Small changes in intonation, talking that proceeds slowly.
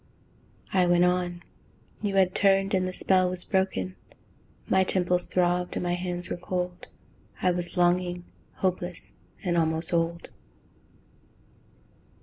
Yes: narrow, 0.8 semitones; slow, 130 wpm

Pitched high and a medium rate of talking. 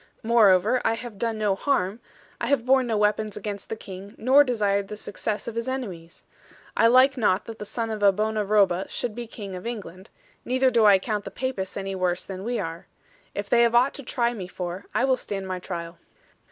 No: high, 215 Hz; fast, 220 wpm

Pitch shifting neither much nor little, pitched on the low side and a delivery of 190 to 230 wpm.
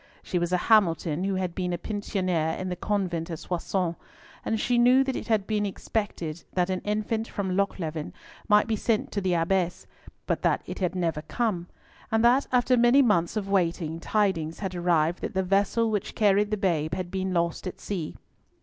No: average, 3.5 semitones; high, 190 Hz; average, 195 wpm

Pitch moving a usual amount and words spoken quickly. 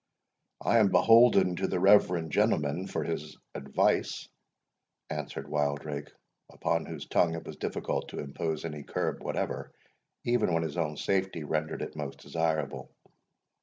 No: average, 3.7 semitones; average, 140 wpm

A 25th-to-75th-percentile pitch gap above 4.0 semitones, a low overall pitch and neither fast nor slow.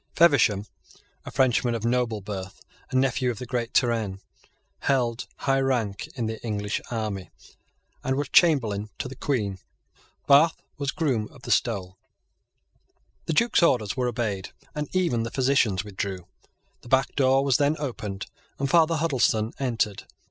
Yes: average, 4.4 semitones; low, 120 Hz; average, 150 wpm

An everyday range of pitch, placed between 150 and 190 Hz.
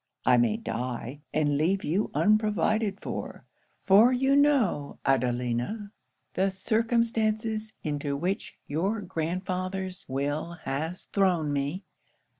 No: wide, 6.9 semitones; medium, 185 Hz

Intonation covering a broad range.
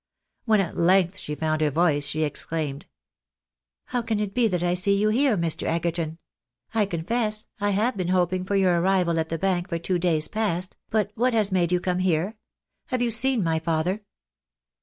No: average, 4.2 semitones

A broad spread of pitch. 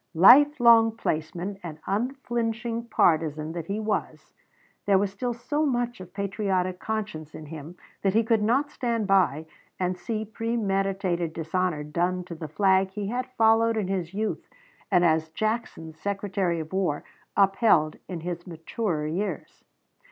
No: average, 4.8 semitones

